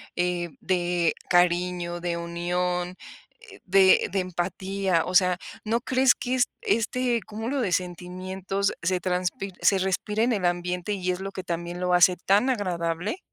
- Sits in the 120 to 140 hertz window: No, medium, 180 Hz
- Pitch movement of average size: No, narrow, 2.0 semitones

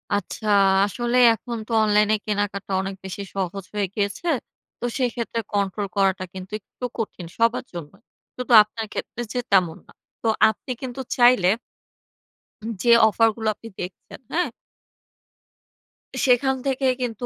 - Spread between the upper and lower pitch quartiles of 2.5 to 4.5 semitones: Yes, average, 3.5 semitones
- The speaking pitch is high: Yes, high, 215 Hz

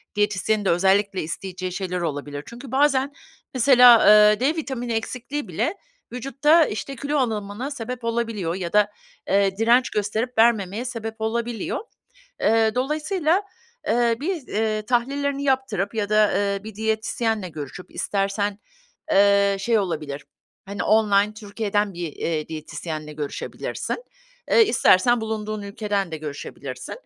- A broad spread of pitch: No, average, 3.8 semitones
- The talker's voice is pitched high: Yes, high, 215 Hz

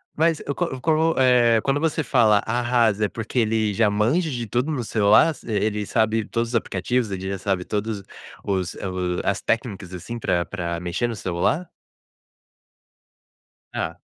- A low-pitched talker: Yes, low, 110 Hz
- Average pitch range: Yes, average, 3.9 semitones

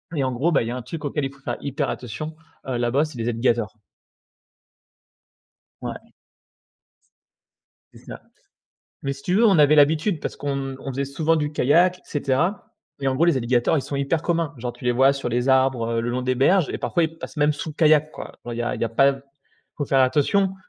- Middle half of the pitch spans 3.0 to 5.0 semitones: Yes, average, 3.5 semitones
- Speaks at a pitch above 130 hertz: Yes, medium, 140 Hz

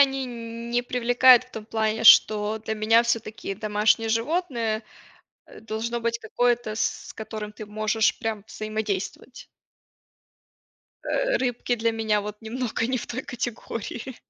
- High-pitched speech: Yes, high, 225 Hz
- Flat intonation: Yes, narrow, 1.9 semitones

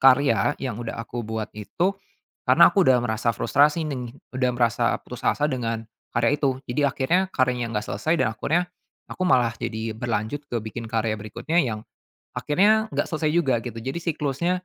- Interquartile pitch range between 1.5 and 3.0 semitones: No, average, 4.7 semitones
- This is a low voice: Yes, low, 125 Hz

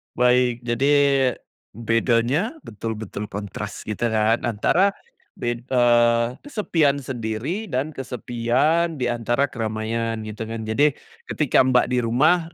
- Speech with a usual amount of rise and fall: Yes, average, 3.6 semitones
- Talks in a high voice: No, low, 120 Hz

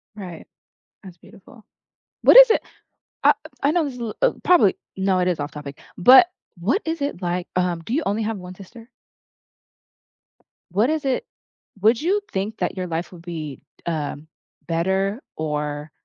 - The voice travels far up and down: Yes, wide, 6.6 semitones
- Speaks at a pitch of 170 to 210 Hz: Yes, high, 190 Hz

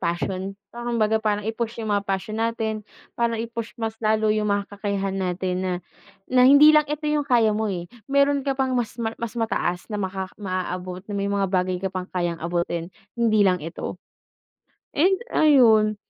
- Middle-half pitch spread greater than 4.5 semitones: No, average, 3.7 semitones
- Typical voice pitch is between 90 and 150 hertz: No, high, 215 Hz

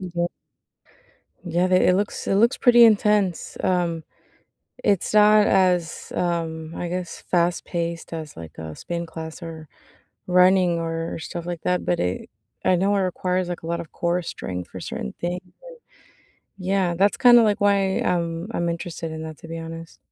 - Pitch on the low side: No, medium, 175 Hz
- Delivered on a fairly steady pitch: Yes, narrow, 2.2 semitones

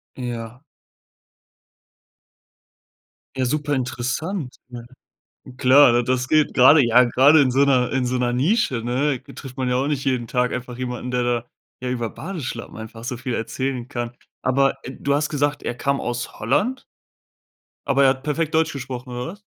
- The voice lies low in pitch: Yes, low, 130 Hz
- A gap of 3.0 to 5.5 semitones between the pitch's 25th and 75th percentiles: No, narrow, 2.5 semitones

